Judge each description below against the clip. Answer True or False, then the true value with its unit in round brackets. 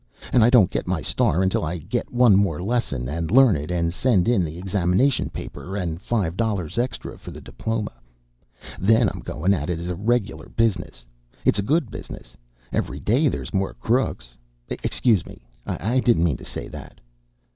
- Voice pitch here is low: True (95 Hz)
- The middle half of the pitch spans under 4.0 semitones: False (5.6 semitones)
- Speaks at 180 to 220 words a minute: True (185 wpm)